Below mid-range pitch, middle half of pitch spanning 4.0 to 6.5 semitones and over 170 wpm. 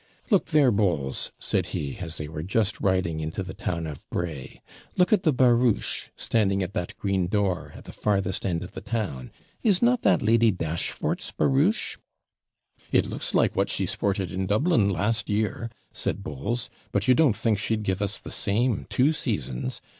Yes: low, 100 Hz; average, 5.0 semitones; average, 180 wpm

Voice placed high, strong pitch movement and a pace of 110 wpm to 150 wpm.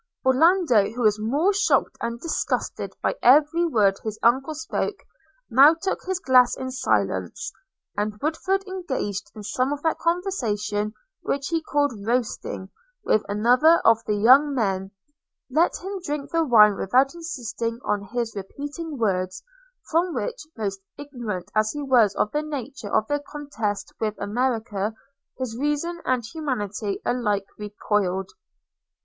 Yes: very high, 250 Hz; wide, 6.1 semitones; average, 145 wpm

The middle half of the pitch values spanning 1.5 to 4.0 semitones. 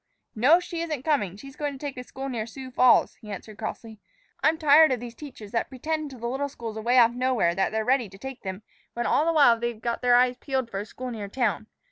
Yes: average, 3.7 semitones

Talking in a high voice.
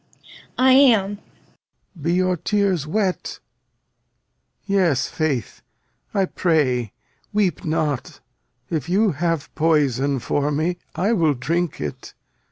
No: medium, 165 Hz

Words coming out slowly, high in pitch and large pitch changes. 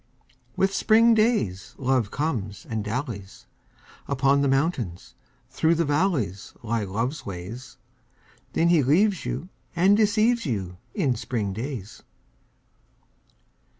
No: slow, 115 wpm; low, 135 Hz; wide, 8.5 semitones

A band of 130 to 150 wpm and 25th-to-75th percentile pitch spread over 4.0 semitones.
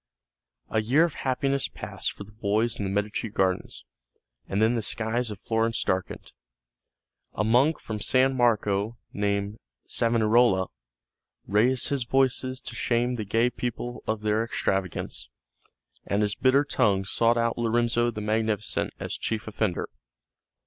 No: average, 140 wpm; average, 2.7 semitones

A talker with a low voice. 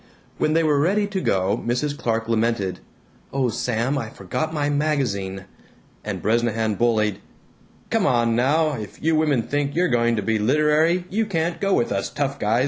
Yes: low, 125 Hz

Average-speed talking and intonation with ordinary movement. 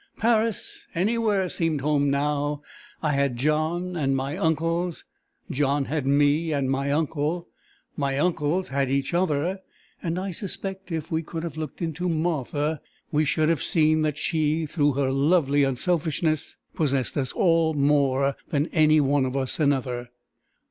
Yes: average, 150 wpm; average, 3.0 semitones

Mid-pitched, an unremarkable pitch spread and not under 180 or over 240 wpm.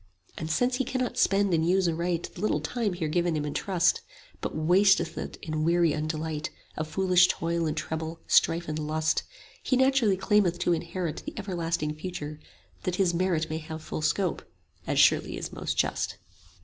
Yes: medium, 170 Hz; average, 3.1 semitones; average, 185 wpm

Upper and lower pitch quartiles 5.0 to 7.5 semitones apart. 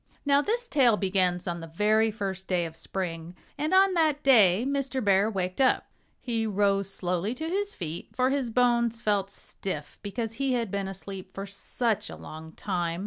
Yes: wide, 5.4 semitones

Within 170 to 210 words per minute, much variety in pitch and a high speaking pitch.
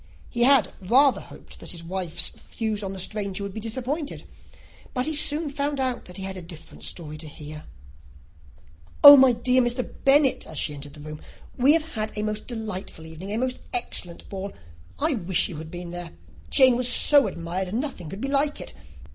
Yes: average, 200 wpm; wide, 6.9 semitones; high, 215 Hz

